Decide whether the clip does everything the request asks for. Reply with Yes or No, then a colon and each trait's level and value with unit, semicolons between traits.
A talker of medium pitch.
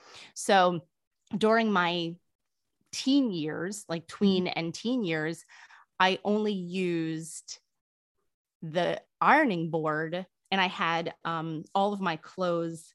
Yes: medium, 175 Hz